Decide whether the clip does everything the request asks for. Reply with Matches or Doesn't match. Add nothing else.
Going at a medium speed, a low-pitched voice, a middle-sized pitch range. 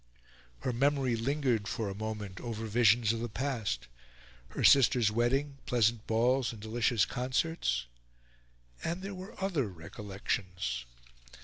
Doesn't match